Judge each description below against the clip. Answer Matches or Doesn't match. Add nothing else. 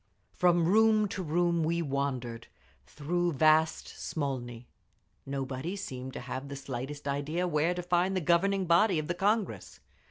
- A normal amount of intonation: Matches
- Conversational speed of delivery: Matches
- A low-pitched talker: Doesn't match